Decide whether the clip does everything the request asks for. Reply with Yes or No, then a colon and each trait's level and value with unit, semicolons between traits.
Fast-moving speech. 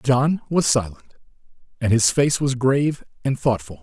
No: average, 155 wpm